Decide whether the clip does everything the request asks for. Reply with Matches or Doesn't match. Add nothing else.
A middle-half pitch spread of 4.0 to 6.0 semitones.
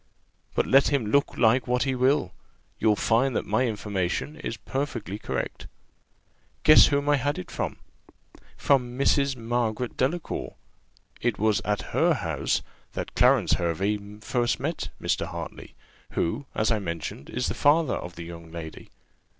Matches